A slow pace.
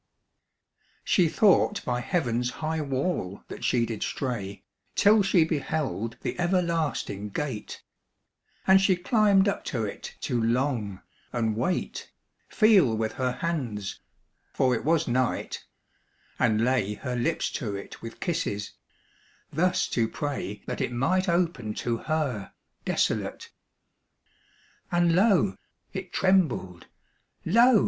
Yes: slow, 125 wpm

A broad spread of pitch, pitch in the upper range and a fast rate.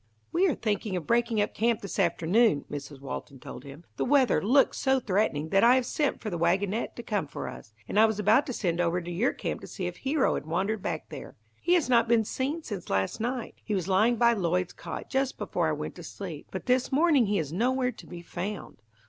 Yes: wide, 6.0 semitones; high, 215 Hz; fast, 240 wpm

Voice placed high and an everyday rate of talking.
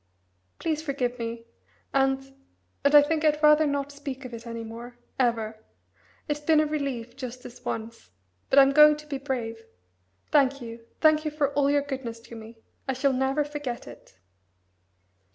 Yes: very high, 270 Hz; average, 170 wpm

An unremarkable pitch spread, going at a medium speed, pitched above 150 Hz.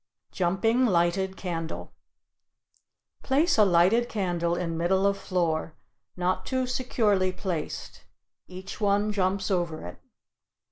No: average, 3.2 semitones; slow, 110 wpm; high, 190 Hz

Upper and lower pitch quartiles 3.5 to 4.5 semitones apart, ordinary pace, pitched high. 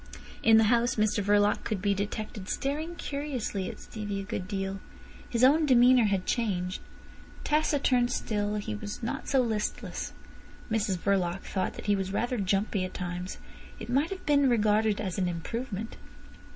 Yes: average, 3.9 semitones; average, 165 wpm; high, 210 Hz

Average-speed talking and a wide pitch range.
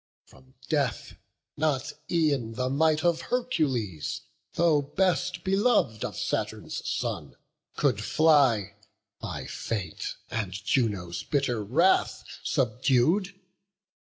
No: slow, 100 wpm; wide, 6.7 semitones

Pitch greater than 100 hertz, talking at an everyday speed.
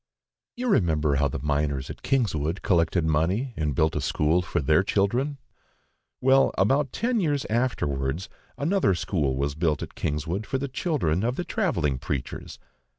No: very low, 90 Hz; average, 155 wpm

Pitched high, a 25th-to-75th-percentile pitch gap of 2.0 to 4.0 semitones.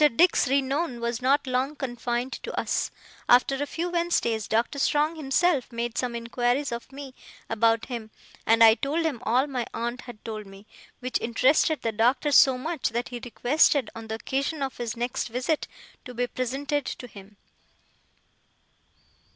Yes: very high, 250 Hz; average, 3.2 semitones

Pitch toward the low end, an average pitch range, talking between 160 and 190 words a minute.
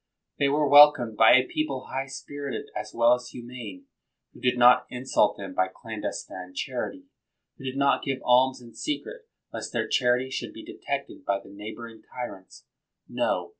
Yes: low, 125 Hz; average, 3.5 semitones; average, 170 wpm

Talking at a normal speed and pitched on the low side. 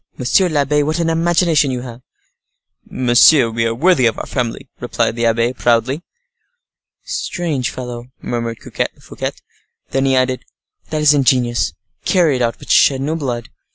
Yes: average, 155 wpm; low, 130 Hz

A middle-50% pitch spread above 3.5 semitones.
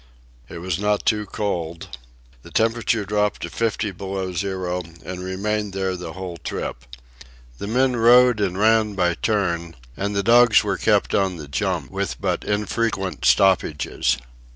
No: average, 2.8 semitones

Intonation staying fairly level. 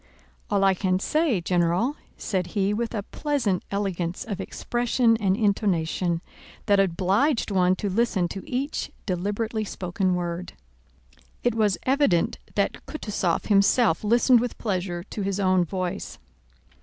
No: average, 3.8 semitones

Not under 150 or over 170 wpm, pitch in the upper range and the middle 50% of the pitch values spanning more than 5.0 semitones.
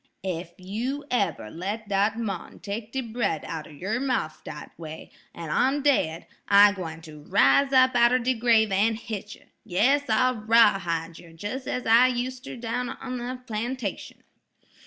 Yes: average, 160 wpm; high, 220 Hz; wide, 5.6 semitones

